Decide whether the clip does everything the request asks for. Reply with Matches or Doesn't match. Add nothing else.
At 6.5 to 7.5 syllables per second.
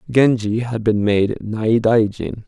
Doesn't match